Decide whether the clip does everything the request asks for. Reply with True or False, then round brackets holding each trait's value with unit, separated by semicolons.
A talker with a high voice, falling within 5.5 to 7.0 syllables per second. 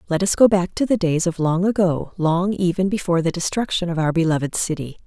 False (175 Hz; 5.9 syllables/s)